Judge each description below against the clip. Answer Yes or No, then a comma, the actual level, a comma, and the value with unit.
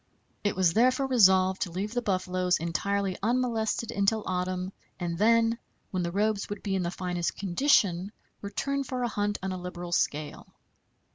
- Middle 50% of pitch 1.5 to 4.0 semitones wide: Yes, average, 3.5 semitones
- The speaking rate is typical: Yes, average, 165 wpm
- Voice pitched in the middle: No, high, 195 Hz